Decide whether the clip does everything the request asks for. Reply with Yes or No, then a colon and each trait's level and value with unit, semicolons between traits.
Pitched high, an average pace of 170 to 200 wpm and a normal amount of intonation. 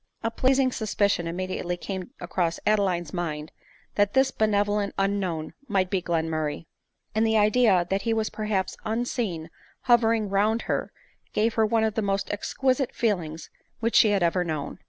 Yes: high, 205 Hz; average, 175 wpm; average, 4.0 semitones